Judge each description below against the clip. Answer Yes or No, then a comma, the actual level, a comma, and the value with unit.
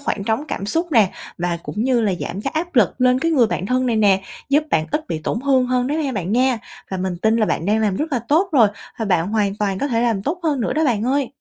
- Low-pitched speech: No, high, 230 Hz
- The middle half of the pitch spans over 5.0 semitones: Yes, wide, 5.5 semitones